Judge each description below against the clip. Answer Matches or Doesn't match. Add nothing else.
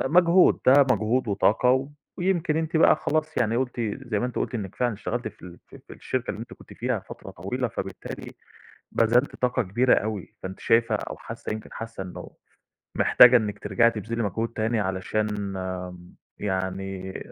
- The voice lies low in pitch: Matches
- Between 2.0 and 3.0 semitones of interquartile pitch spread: Doesn't match